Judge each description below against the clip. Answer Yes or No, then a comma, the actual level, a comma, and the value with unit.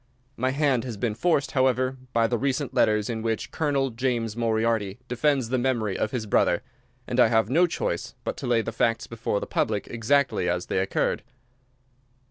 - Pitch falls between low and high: No, low, 120 Hz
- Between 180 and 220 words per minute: Yes, average, 185 wpm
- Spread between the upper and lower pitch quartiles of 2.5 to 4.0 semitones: Yes, average, 2.8 semitones